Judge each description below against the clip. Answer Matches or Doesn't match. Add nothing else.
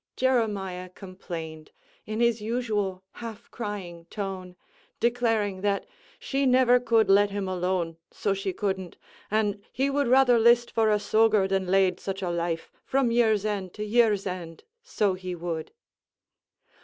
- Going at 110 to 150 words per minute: Matches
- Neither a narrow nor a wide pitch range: Matches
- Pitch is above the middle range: Matches